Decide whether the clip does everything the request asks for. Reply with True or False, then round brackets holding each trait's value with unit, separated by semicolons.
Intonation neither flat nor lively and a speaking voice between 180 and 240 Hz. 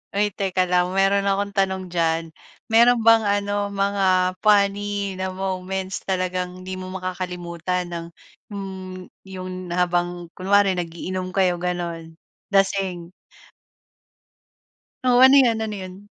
False (1.8 semitones; 185 Hz)